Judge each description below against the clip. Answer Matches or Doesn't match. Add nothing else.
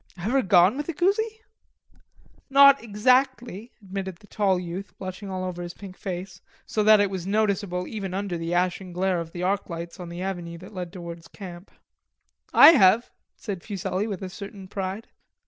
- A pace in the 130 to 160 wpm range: Doesn't match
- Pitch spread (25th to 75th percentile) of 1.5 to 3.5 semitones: Matches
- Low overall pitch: Doesn't match